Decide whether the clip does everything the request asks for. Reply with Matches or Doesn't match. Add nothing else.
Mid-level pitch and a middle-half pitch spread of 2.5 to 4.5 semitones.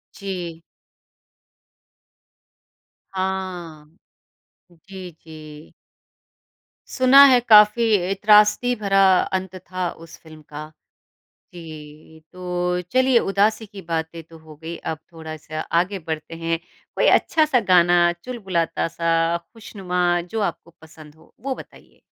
Matches